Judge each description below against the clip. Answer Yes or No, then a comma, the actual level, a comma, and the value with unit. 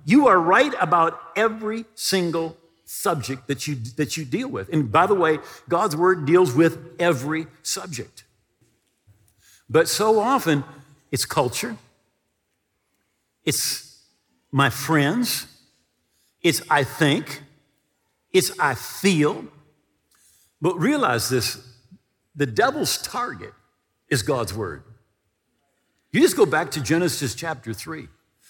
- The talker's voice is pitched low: No, medium, 155 Hz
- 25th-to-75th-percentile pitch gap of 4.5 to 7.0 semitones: Yes, average, 5.3 semitones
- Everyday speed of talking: No, slow, 115 wpm